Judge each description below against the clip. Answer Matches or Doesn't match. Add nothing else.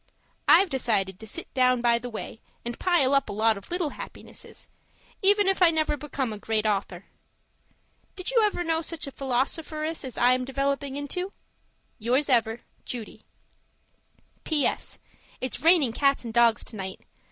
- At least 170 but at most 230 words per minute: Doesn't match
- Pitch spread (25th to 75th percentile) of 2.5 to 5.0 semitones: Doesn't match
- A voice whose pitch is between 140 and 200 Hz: Doesn't match